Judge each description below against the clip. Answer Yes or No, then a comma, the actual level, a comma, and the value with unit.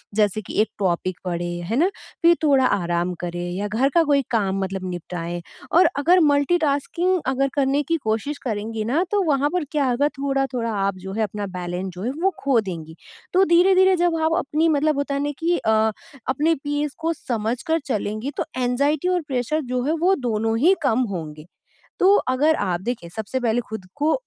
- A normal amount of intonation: No, wide, 7.1 semitones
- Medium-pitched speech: No, very high, 255 Hz